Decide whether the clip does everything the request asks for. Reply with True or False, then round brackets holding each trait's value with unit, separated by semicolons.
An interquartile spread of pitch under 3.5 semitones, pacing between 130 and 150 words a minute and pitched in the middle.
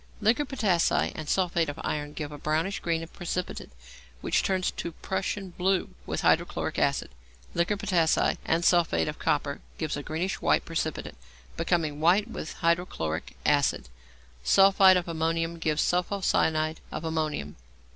True (3.0 semitones; 145 wpm; 170 Hz)